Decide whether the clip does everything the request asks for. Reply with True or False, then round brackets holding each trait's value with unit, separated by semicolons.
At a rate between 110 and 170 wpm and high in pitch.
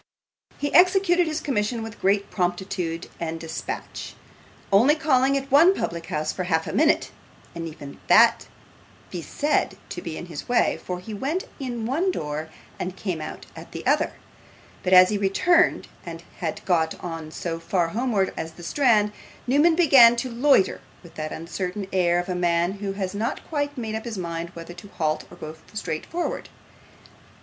False (180 wpm; 195 Hz)